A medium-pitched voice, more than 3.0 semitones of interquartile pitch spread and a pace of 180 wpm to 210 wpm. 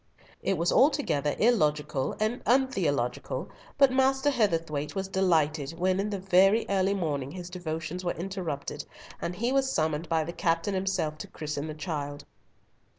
No: medium, 175 Hz; average, 4.6 semitones; average, 150 wpm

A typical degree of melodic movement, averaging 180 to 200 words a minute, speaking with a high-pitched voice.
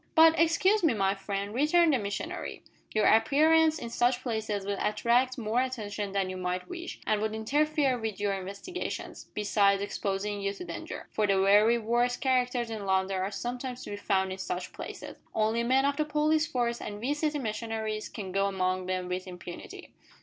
Yes: average, 4.6 semitones; average, 185 wpm; high, 220 Hz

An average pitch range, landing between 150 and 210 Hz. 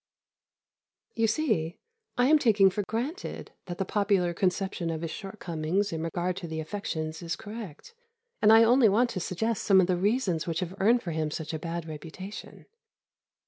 Yes: average, 4.7 semitones; high, 190 Hz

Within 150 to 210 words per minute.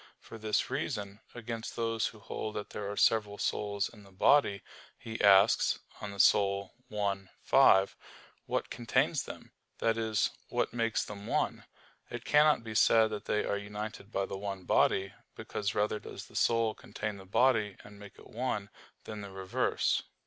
Yes: average, 170 wpm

